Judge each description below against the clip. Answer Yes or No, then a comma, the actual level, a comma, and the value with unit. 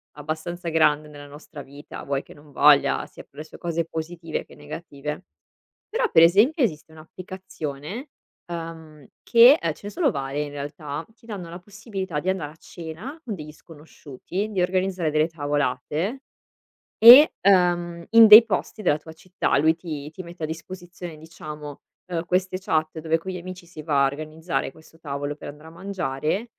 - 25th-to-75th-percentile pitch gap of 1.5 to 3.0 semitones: No, average, 3.7 semitones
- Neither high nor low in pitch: Yes, medium, 165 Hz